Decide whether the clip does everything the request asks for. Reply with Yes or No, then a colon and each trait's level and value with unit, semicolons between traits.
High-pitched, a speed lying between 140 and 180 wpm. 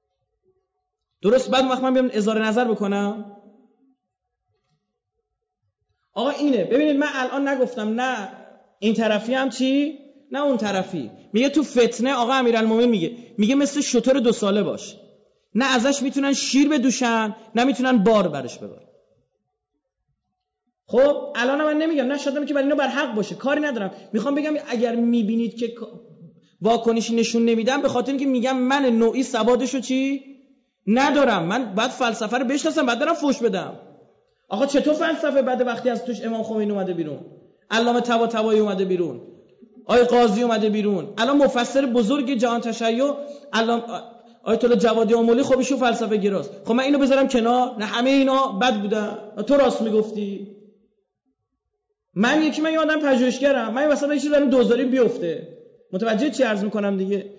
Yes: high, 245 Hz; fast, 155 wpm